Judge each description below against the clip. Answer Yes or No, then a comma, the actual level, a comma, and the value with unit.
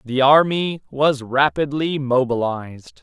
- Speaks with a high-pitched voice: No, low, 135 Hz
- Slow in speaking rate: Yes, slow, 100 wpm